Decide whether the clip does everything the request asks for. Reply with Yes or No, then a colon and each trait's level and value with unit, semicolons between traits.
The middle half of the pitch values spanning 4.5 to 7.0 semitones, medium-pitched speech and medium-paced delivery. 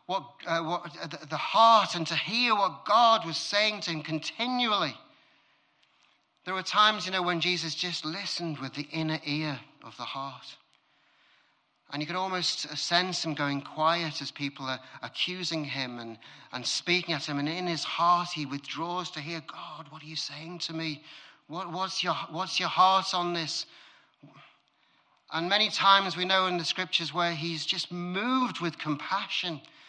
No: average, 3.3 semitones; medium, 170 Hz; average, 175 wpm